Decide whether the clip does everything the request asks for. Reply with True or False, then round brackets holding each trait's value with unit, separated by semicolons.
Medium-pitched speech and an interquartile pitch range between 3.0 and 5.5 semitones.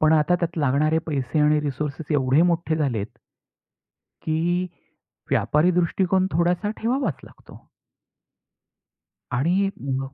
True (155 Hz; 3.6 semitones)